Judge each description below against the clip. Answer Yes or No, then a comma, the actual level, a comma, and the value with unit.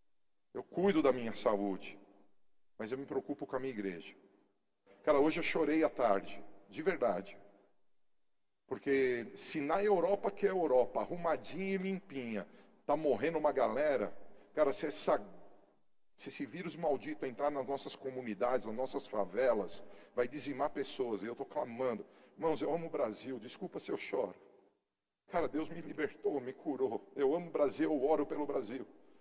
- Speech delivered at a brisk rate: No, average, 165 wpm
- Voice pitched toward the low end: Yes, low, 125 Hz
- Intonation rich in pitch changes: Yes, wide, 6.3 semitones